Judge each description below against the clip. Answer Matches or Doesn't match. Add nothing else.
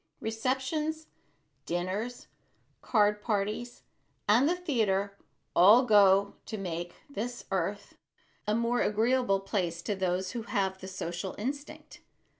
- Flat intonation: Doesn't match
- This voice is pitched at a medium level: Doesn't match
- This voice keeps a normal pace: Doesn't match